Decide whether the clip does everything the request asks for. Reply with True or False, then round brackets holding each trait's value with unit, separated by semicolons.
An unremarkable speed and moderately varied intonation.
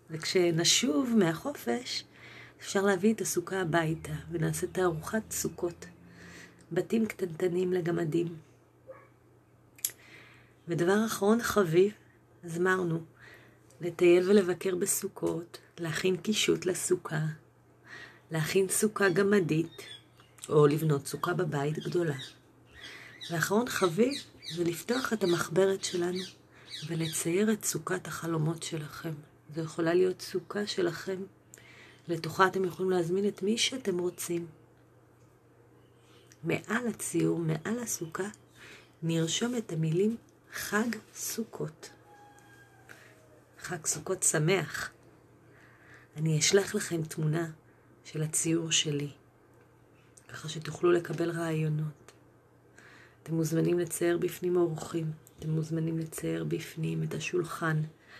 False (95 wpm; 3.1 semitones)